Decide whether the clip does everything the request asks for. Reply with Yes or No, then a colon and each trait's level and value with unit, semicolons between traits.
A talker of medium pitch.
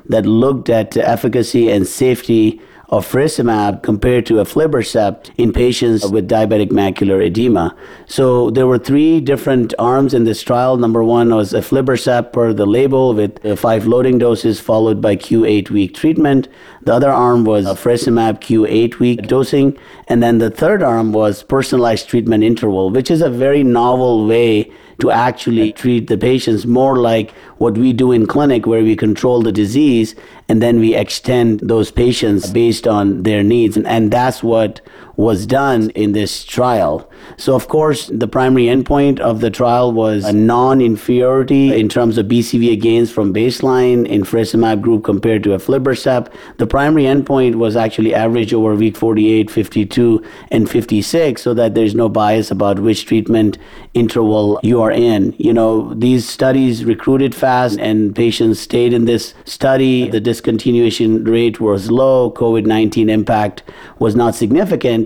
No: low, 115 Hz